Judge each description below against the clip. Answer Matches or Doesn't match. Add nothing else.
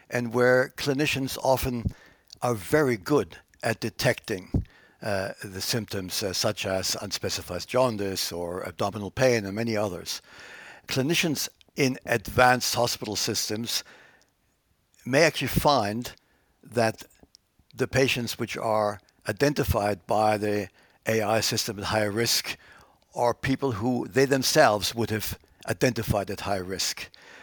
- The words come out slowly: Matches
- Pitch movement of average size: Matches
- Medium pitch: Doesn't match